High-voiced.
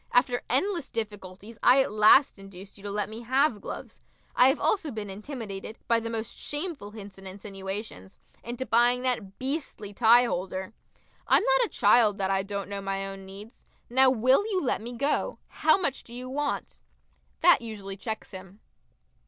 Yes: high, 225 Hz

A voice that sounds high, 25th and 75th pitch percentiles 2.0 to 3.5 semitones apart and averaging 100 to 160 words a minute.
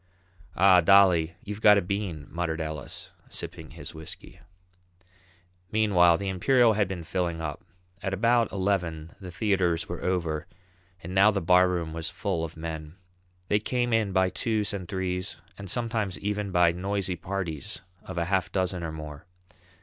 No: very low, 90 Hz; average, 3.1 semitones; average, 155 wpm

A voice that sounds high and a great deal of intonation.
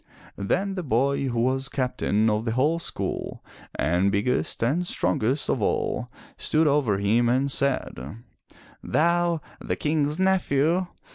No: low, 135 Hz; wide, 5.7 semitones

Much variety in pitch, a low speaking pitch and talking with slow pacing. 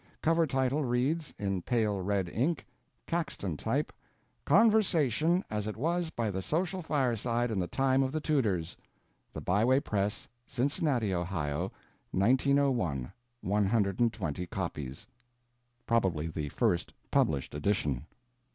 Yes: wide, 7.2 semitones; low, 115 Hz; slow, 120 wpm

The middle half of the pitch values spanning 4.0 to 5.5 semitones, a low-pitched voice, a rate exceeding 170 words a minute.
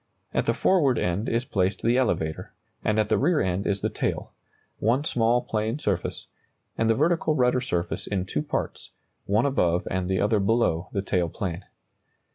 Yes: average, 5.0 semitones; low, 105 Hz; average, 180 wpm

